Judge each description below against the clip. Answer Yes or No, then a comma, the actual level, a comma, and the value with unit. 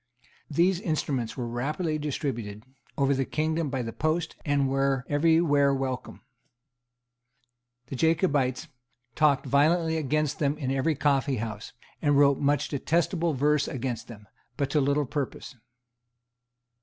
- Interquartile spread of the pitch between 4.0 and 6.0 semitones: No, average, 2.7 semitones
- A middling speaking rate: No, slow, 130 wpm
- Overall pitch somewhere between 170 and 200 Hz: No, medium, 140 Hz